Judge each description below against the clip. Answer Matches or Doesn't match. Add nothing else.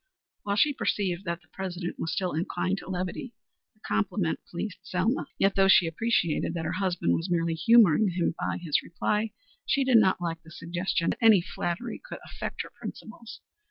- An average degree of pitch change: Matches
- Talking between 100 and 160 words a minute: Doesn't match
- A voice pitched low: Doesn't match